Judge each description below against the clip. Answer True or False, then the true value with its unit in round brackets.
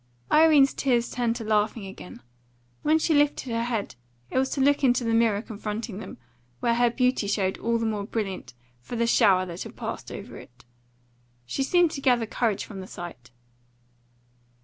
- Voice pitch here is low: False (230 Hz)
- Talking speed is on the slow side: False (180 wpm)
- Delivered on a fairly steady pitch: False (4.0 semitones)